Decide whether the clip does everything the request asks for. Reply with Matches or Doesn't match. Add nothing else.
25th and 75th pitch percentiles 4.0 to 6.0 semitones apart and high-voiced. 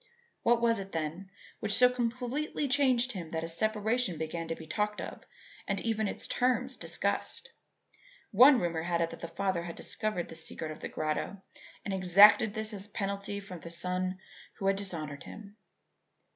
Matches